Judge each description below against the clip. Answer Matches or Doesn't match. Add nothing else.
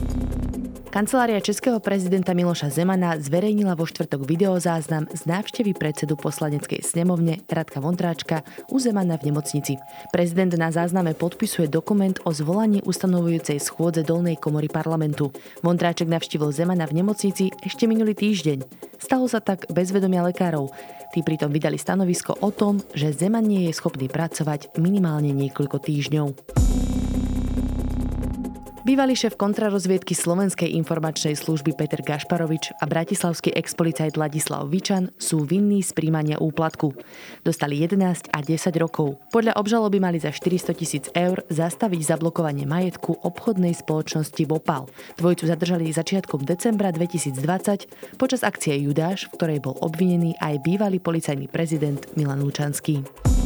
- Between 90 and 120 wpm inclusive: Doesn't match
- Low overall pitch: Doesn't match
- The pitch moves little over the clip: Doesn't match